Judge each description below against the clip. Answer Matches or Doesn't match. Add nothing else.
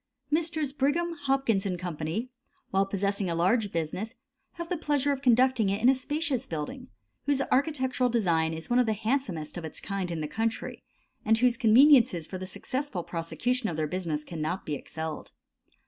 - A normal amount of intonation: Doesn't match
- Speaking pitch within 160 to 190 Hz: Doesn't match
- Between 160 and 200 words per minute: Matches